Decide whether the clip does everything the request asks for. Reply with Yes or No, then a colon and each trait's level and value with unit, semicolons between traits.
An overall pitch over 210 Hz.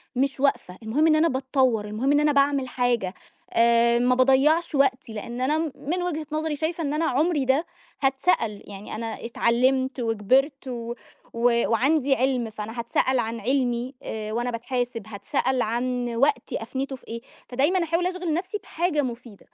Yes: very high, 260 Hz